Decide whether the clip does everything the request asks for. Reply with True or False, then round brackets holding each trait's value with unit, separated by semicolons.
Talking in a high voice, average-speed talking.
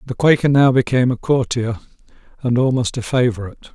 False (125 Hz; 160 wpm)